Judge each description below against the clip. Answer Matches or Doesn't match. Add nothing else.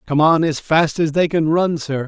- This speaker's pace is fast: Matches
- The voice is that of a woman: Doesn't match